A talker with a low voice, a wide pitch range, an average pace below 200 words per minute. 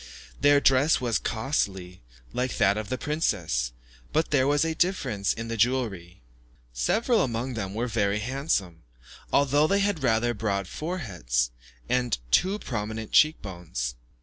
Yes: low, 115 Hz; wide, 6.5 semitones; average, 145 wpm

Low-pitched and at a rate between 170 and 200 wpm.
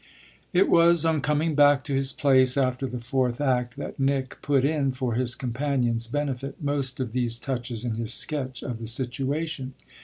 Yes: low, 130 Hz; average, 180 wpm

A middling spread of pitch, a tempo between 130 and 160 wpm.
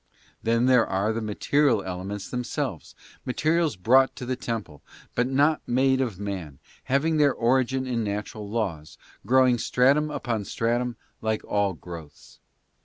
Yes: average, 4.4 semitones; average, 145 wpm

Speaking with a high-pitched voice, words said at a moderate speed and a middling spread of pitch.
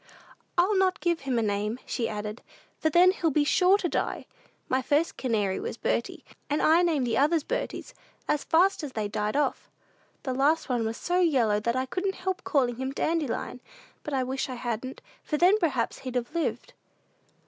No: very high, 275 Hz; average, 190 wpm; wide, 6.0 semitones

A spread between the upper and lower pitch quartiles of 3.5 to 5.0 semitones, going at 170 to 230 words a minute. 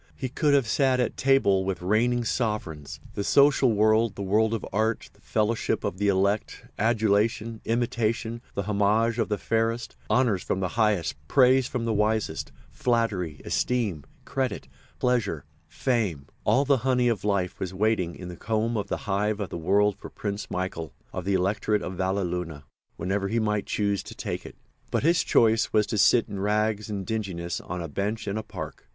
No: average, 3.1 semitones; average, 180 wpm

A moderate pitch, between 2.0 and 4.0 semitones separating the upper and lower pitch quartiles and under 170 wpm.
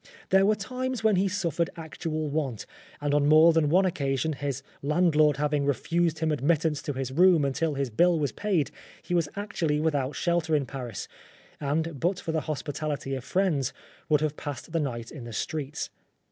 No: medium, 155 Hz; average, 3.2 semitones; average, 185 wpm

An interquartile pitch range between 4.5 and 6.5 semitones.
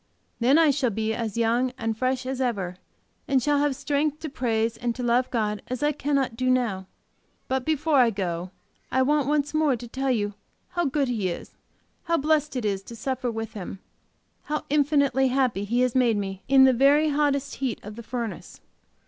No: average, 3.9 semitones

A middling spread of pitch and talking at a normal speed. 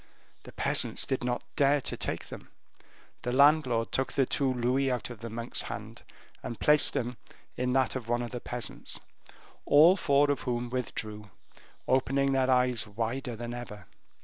No: narrow, 2.2 semitones; average, 170 wpm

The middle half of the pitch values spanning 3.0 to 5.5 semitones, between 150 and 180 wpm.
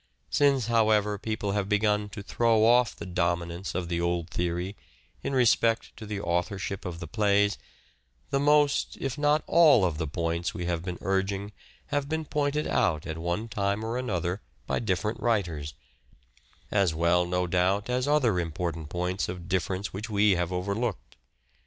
Yes: average, 4.5 semitones; average, 165 wpm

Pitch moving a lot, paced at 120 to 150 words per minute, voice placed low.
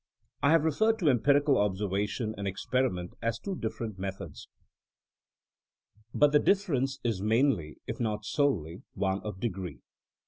Yes: wide, 6.6 semitones; average, 140 wpm; low, 110 Hz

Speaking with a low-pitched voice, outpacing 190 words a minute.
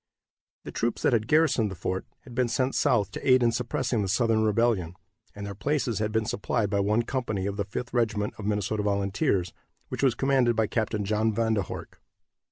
Yes: low, 110 Hz; fast, 205 wpm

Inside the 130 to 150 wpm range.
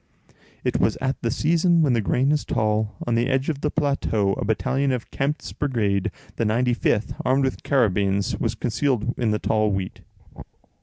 No: average, 175 wpm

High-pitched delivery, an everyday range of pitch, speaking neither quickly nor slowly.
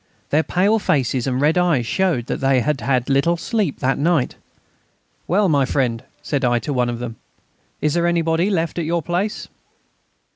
No: medium, 150 Hz; average, 4.9 semitones; average, 180 wpm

